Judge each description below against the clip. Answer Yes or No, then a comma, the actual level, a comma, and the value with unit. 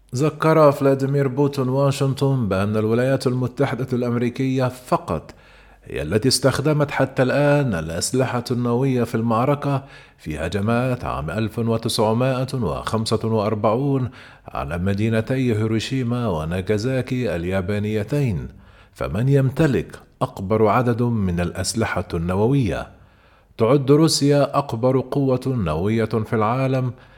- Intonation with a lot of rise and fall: No, average, 3.7 semitones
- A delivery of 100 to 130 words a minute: No, average, 90 wpm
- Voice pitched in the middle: No, low, 125 Hz